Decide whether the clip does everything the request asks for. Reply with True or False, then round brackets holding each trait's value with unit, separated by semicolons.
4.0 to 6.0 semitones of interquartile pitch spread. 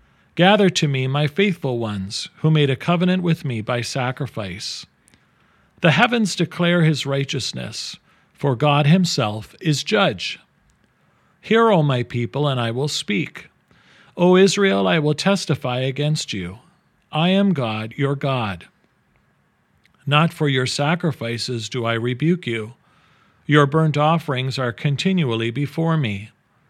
True (5.1 semitones)